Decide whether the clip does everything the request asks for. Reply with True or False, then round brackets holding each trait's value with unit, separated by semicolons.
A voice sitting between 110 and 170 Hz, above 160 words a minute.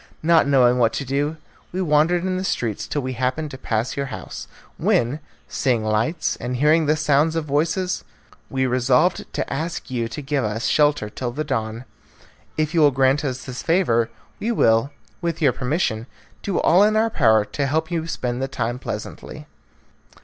True (140 Hz; 185 wpm)